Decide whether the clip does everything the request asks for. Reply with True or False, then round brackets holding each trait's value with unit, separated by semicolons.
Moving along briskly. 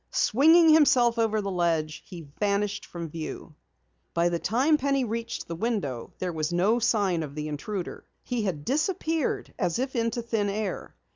False (165 wpm)